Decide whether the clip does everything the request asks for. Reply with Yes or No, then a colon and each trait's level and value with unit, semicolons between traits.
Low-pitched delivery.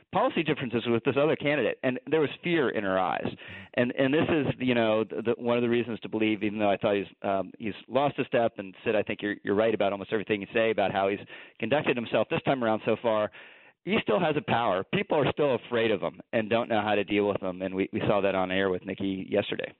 Yes: low, 110 Hz